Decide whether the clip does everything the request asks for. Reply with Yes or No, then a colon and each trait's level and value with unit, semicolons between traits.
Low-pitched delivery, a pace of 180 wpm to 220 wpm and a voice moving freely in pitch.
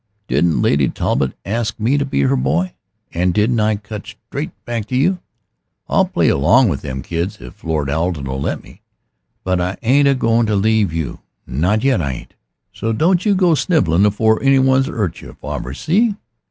Yes: low, 105 Hz; average, 190 wpm; wide, 8.0 semitones